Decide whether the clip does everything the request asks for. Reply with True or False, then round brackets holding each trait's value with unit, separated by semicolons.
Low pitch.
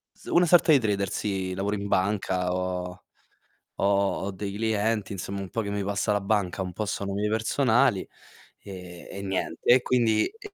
True (100 Hz)